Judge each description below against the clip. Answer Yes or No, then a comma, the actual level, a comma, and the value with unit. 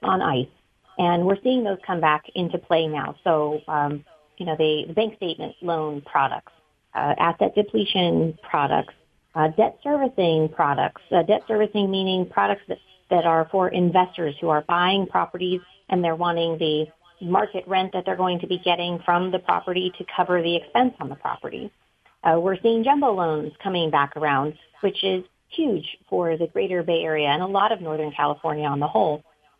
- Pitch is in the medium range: Yes, medium, 175 Hz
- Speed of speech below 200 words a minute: Yes, average, 180 wpm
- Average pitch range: Yes, average, 3.2 semitones